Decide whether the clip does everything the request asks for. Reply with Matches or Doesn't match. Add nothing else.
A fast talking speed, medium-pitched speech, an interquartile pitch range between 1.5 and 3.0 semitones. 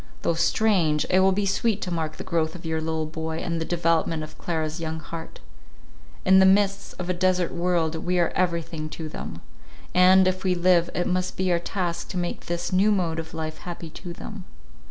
Matches